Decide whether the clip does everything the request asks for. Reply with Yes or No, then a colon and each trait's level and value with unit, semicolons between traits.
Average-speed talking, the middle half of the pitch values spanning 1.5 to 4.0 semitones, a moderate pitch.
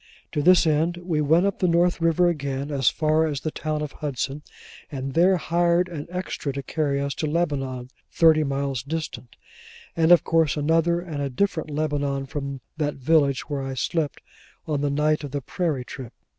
Yes: average, 185 wpm; average, 3.0 semitones; medium, 150 Hz